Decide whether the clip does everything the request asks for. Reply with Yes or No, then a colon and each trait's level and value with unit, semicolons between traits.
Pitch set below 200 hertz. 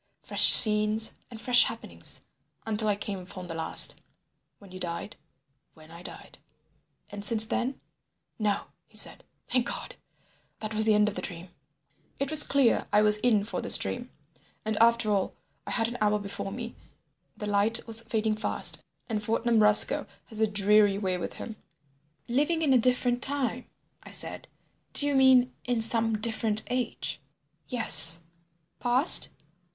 No: high, 220 Hz